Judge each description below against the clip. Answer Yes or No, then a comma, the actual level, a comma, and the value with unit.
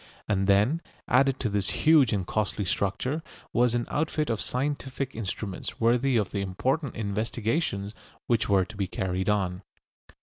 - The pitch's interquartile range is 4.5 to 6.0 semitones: Yes, average, 4.8 semitones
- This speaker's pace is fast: No, average, 155 wpm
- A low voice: Yes, low, 110 Hz